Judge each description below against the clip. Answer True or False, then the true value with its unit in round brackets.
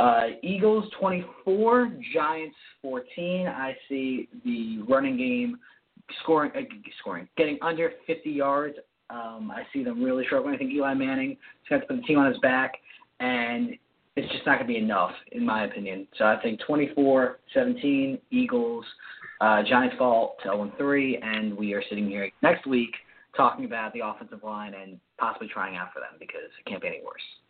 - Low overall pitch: False (160 Hz)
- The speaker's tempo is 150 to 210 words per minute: True (175 wpm)